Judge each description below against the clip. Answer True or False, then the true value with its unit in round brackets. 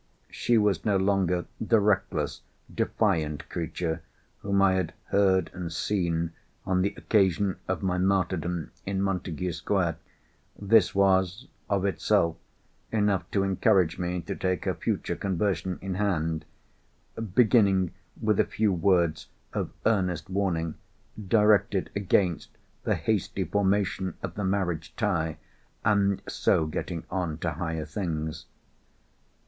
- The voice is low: True (95 Hz)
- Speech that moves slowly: True (125 wpm)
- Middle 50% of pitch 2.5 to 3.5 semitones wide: True (2.9 semitones)